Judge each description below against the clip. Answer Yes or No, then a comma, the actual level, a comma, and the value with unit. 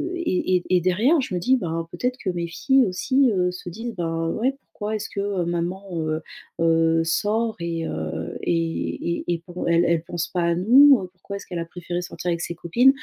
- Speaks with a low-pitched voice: No, medium, 180 Hz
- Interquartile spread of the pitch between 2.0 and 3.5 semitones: No, average, 4.2 semitones